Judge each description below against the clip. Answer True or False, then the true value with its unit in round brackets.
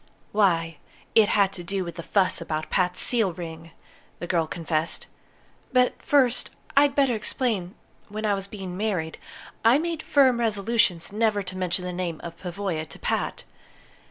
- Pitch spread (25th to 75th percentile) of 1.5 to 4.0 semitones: False (4.5 semitones)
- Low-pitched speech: False (195 Hz)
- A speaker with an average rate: True (165 wpm)